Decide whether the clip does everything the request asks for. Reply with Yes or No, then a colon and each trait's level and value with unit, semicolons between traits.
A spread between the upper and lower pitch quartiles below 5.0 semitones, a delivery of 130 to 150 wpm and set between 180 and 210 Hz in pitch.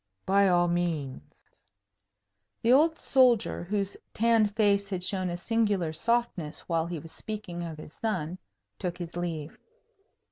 Yes: average, 3.9 semitones; average, 140 wpm; medium, 185 Hz